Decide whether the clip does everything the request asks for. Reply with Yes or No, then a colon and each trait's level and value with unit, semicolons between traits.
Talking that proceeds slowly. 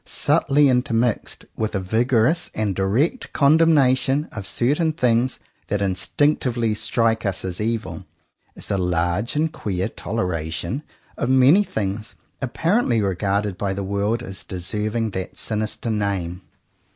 Yes: slow, 125 wpm